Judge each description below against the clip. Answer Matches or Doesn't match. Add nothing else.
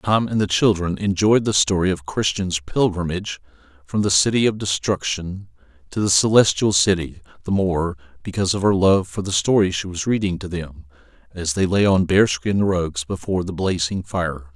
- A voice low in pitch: Matches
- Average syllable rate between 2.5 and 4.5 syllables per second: Doesn't match